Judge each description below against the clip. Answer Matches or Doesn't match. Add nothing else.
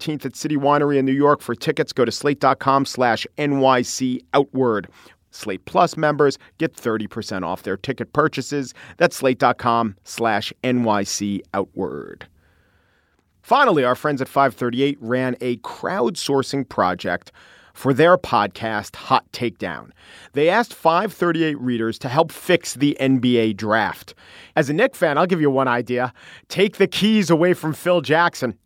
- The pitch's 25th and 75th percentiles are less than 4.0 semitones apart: Doesn't match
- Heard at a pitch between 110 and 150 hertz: Matches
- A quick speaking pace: Doesn't match